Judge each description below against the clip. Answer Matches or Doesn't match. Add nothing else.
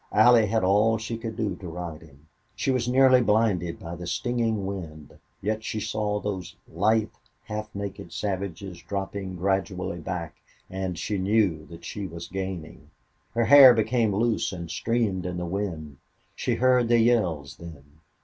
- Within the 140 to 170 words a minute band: Matches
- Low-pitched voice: Matches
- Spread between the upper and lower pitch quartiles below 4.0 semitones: Doesn't match